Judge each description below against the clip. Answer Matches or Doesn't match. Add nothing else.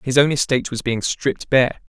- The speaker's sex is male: Matches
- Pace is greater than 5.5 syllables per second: Matches